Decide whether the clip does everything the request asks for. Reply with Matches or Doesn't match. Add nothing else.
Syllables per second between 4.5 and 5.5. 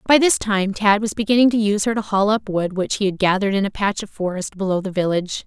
Doesn't match